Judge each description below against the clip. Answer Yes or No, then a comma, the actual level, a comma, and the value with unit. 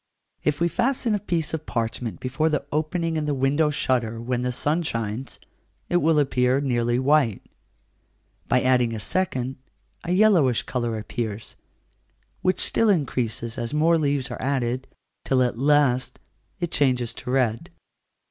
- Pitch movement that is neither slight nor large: Yes, average, 4.3 semitones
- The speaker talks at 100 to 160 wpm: Yes, average, 150 wpm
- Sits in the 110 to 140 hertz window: Yes, low, 135 Hz